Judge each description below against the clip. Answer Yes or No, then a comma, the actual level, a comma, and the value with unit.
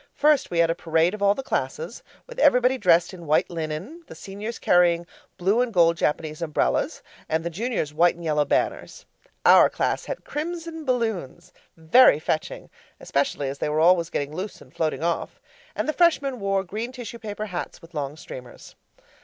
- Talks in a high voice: No, medium, 175 Hz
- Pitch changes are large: Yes, wide, 6.8 semitones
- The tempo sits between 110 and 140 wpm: No, average, 180 wpm